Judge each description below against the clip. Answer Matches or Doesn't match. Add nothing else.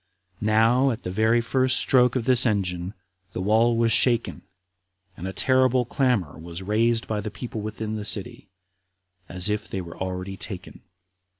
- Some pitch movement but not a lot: Matches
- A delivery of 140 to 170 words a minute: Matches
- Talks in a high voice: Doesn't match